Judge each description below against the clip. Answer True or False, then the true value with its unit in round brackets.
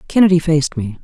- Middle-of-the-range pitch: True (155 Hz)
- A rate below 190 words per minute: True (175 wpm)